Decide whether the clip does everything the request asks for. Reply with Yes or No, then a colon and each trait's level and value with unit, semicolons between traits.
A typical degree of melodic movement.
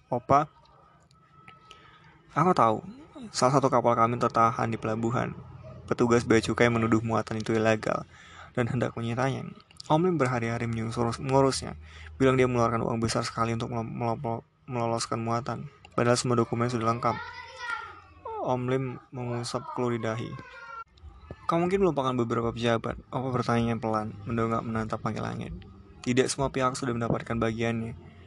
No: narrow, 2.3 semitones